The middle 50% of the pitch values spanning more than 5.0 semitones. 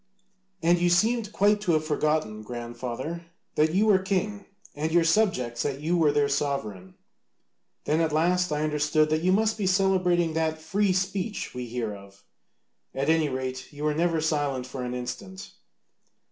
Yes: wide, 5.4 semitones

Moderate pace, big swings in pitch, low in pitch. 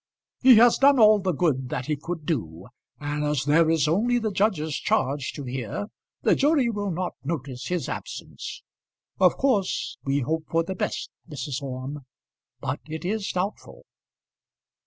No: average, 160 wpm; wide, 6.2 semitones; medium, 160 Hz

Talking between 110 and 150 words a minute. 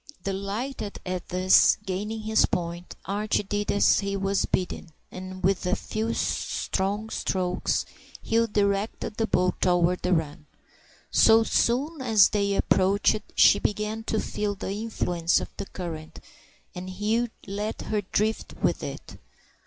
Yes: average, 140 wpm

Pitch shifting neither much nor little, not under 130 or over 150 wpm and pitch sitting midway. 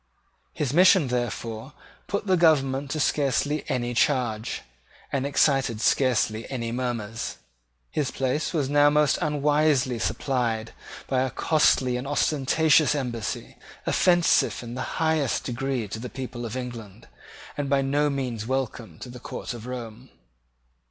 No: average, 3.3 semitones; average, 140 wpm; low, 130 Hz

